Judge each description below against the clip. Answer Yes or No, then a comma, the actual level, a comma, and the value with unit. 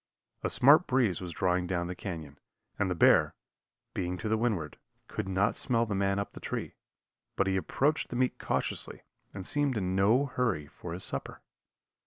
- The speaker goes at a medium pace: Yes, average, 185 wpm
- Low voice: Yes, very low, 95 Hz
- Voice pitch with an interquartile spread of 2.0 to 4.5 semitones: No, average, 4.9 semitones